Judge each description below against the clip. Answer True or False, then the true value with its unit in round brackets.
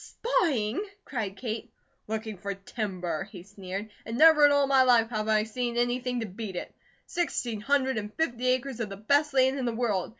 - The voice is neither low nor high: False (230 Hz)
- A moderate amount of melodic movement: True (3.8 semitones)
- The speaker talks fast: False (195 wpm)